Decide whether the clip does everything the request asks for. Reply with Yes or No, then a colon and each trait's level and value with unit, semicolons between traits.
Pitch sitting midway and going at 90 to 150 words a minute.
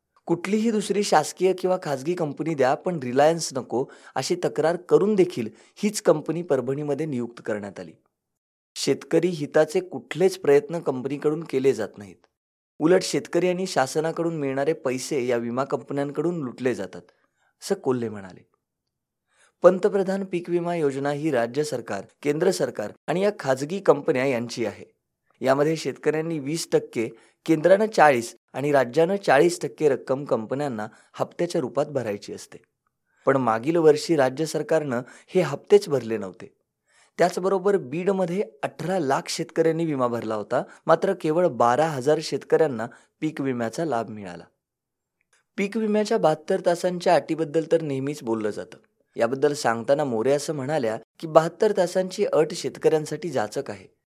Yes: medium, 155 Hz; slow, 135 wpm